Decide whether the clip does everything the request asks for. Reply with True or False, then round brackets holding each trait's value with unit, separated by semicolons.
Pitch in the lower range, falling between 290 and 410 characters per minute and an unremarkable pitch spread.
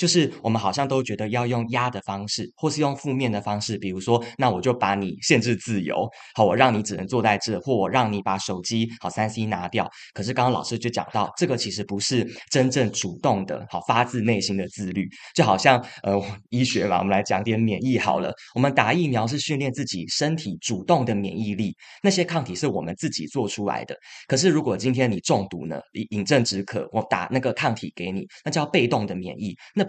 True (115 Hz; 325 characters per minute; 4.5 semitones)